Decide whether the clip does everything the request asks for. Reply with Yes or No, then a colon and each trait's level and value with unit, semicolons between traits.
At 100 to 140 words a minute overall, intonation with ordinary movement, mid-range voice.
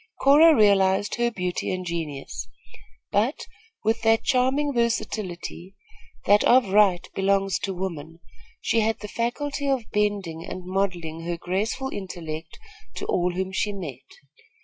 No: slow, 135 wpm; average, 4.3 semitones; high, 195 Hz